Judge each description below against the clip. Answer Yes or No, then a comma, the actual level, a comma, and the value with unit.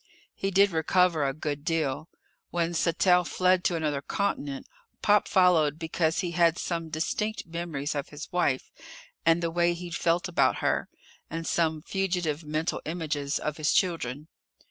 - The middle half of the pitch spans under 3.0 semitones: Yes, narrow, 2.5 semitones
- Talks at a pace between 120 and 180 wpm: Yes, average, 155 wpm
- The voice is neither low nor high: Yes, medium, 165 Hz